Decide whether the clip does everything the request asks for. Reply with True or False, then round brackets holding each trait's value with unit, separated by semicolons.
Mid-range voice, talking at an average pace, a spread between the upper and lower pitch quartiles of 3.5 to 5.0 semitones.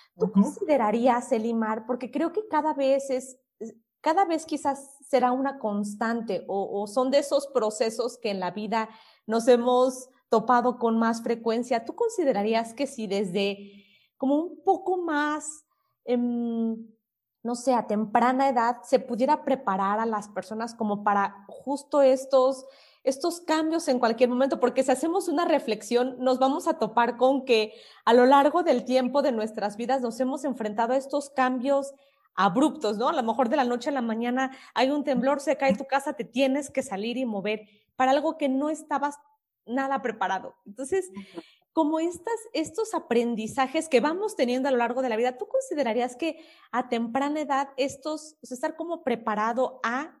False (260 Hz; 170 wpm; 3.9 semitones)